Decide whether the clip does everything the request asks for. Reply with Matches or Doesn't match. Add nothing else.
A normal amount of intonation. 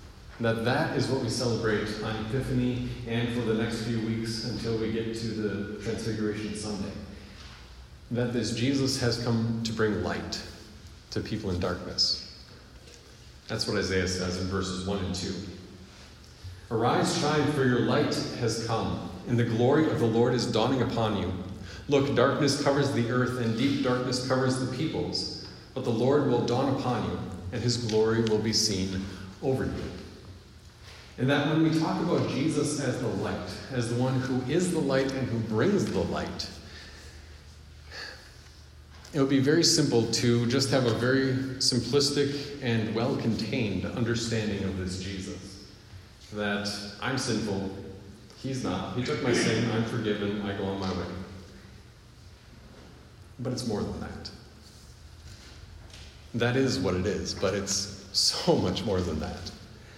Matches